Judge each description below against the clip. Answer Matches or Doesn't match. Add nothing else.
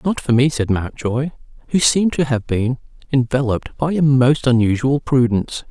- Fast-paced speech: Doesn't match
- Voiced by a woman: Doesn't match